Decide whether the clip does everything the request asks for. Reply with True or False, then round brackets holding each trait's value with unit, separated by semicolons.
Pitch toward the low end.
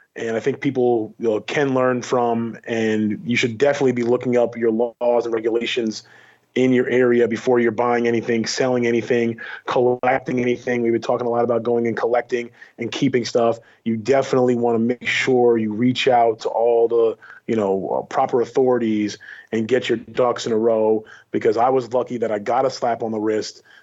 True (120 Hz)